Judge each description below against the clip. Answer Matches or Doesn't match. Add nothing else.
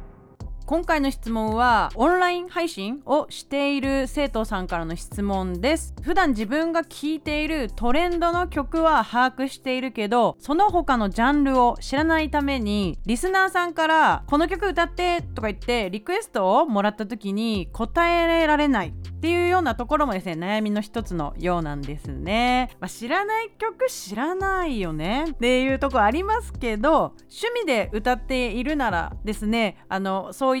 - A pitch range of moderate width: Doesn't match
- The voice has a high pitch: Matches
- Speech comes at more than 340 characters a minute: Matches